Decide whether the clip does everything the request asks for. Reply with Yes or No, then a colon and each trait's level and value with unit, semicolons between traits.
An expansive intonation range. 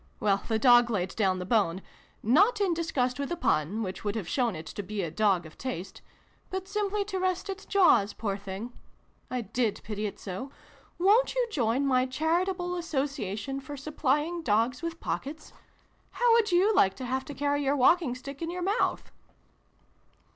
Yes: wide, 8.6 semitones